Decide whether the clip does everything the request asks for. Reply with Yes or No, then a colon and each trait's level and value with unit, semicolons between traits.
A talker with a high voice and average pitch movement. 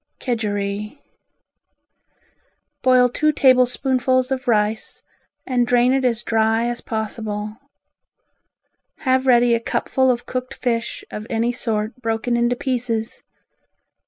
No: high, 240 Hz; narrow, 2.3 semitones